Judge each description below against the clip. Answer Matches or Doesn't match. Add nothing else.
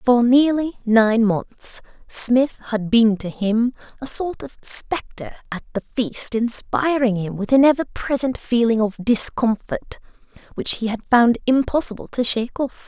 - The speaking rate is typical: Matches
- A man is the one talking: Doesn't match